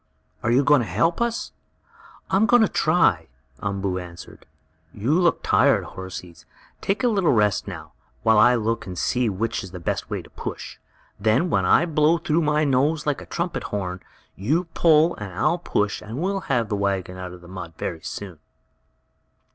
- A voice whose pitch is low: Yes, low, 115 Hz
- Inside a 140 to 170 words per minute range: No, average, 185 wpm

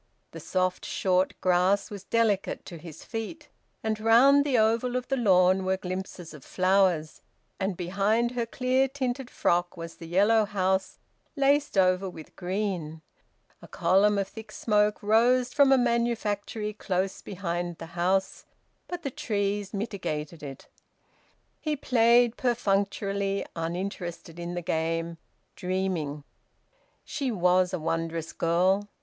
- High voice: Yes, high, 195 Hz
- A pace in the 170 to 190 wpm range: No, slow, 135 wpm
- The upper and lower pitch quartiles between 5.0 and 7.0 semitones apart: No, average, 4.3 semitones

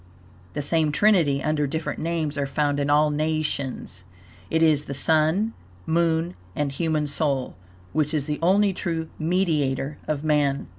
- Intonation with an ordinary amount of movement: No, narrow, 2.2 semitones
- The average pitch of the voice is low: No, medium, 155 Hz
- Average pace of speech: Yes, average, 150 wpm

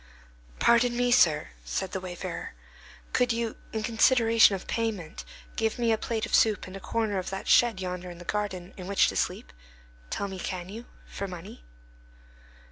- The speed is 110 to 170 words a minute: No, average, 180 wpm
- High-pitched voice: Yes, high, 200 Hz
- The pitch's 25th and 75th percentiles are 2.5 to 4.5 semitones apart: Yes, average, 3.9 semitones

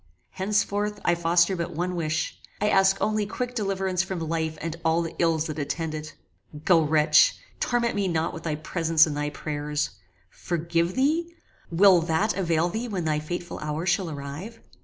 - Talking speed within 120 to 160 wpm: No, average, 175 wpm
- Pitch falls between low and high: Yes, medium, 170 Hz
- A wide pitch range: No, average, 3.5 semitones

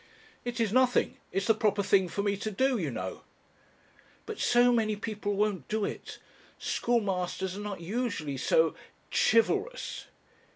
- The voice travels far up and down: No, average, 3.6 semitones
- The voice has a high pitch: Yes, high, 210 Hz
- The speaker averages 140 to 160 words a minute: Yes, average, 150 wpm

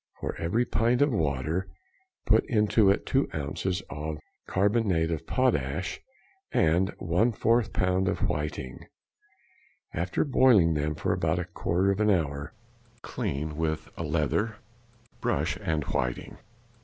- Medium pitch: No, very low, 90 Hz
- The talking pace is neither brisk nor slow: No, slow, 130 wpm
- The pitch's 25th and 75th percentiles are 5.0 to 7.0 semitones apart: Yes, wide, 5.6 semitones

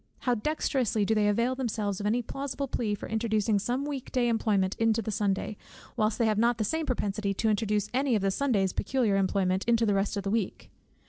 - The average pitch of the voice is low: No, high, 220 Hz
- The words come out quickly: Yes, fast, 210 wpm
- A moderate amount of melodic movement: Yes, average, 3.1 semitones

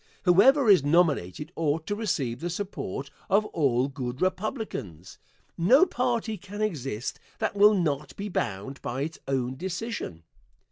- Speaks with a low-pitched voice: No, medium, 165 Hz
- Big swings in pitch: Yes, wide, 7.4 semitones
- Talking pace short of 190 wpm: Yes, average, 140 wpm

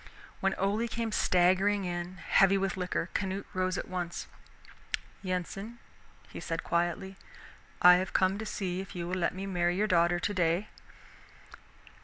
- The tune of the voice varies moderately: No, narrow, 1.9 semitones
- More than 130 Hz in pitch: Yes, medium, 185 Hz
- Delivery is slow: No, average, 150 wpm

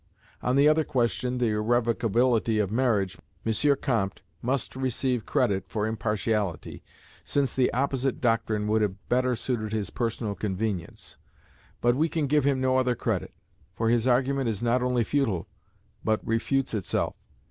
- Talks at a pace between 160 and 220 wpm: No, average, 150 wpm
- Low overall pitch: Yes, low, 120 Hz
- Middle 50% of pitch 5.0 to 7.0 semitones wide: No, average, 3.3 semitones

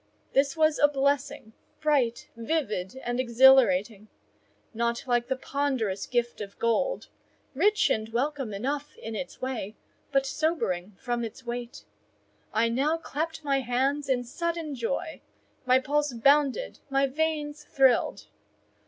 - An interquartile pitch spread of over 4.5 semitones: No, average, 3.8 semitones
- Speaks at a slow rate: Yes, slow, 125 wpm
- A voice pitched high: Yes, very high, 265 Hz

